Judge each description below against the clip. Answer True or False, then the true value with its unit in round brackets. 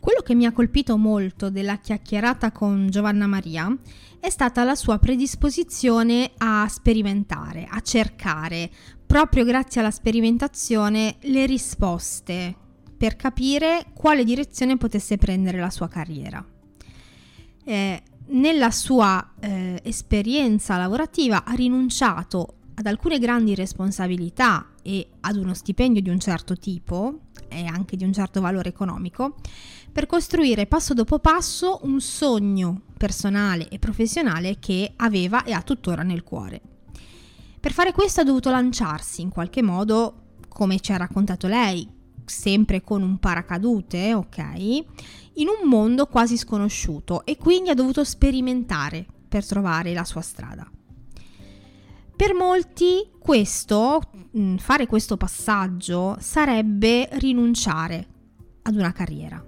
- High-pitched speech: True (215 Hz)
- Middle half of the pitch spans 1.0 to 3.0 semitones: False (5.5 semitones)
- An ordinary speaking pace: True (125 wpm)